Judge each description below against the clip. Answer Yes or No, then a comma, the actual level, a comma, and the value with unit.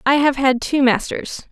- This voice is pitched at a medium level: No, very high, 265 Hz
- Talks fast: No, average, 195 wpm